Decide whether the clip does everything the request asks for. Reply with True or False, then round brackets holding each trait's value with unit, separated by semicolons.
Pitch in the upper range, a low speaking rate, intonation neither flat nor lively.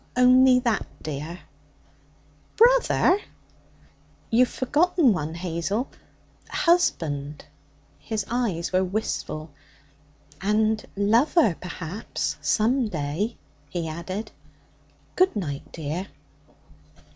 False (205 Hz; 80 wpm; 7.1 semitones)